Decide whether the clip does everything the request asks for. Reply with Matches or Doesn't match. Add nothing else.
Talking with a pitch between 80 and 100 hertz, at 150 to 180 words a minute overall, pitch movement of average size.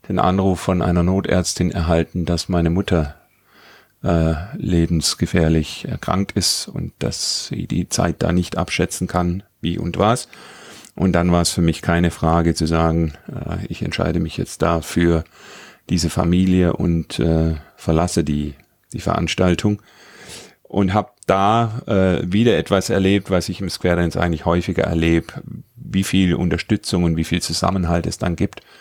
Doesn't match